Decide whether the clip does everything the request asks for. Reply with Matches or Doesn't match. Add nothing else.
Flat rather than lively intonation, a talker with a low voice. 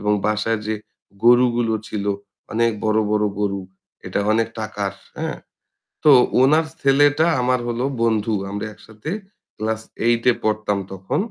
Matches